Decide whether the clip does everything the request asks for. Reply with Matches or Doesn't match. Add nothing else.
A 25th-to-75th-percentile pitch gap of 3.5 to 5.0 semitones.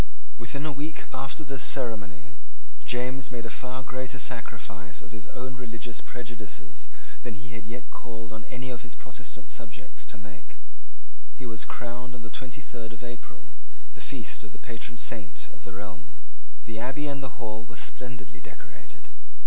Doesn't match